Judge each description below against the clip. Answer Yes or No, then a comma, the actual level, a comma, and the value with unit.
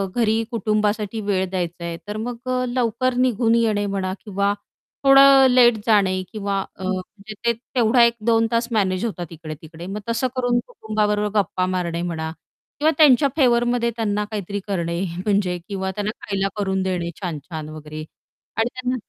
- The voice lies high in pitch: Yes, high, 210 Hz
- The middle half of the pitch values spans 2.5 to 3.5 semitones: No, average, 4.0 semitones